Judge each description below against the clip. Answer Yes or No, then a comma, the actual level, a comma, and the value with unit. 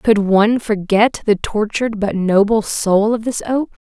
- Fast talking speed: No, average, 170 wpm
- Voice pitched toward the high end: Yes, high, 215 Hz